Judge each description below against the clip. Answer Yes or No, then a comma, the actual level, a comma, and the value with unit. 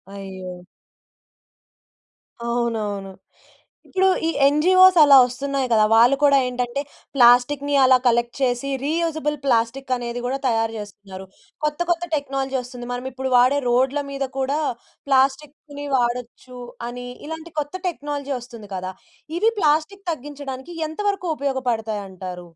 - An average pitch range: Yes, average, 3.3 semitones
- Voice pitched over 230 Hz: Yes, very high, 265 Hz